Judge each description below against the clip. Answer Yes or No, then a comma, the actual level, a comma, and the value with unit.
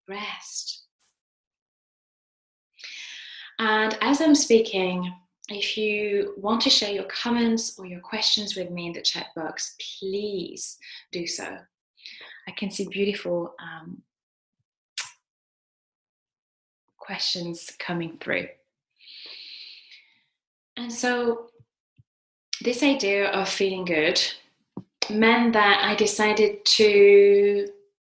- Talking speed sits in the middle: No, slow, 95 wpm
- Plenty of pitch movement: No, average, 4.5 semitones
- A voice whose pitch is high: Yes, high, 205 Hz